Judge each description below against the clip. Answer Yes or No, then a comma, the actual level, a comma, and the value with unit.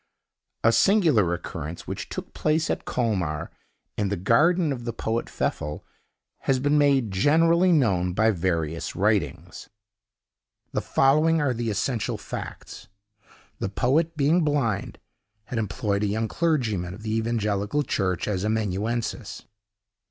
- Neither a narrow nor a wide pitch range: No, wide, 6.6 semitones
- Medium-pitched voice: No, low, 110 Hz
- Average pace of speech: No, slow, 130 wpm